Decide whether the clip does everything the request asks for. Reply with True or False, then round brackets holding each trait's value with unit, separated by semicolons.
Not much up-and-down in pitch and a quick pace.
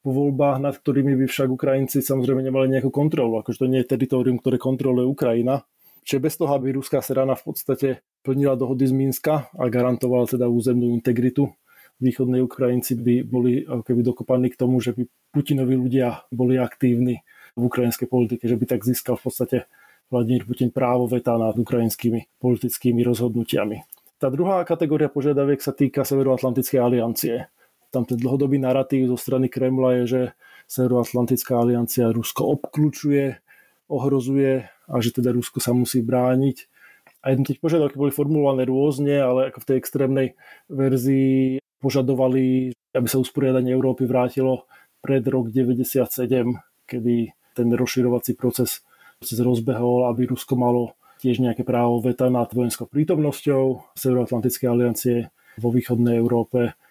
False (1.5 semitones; 140 wpm)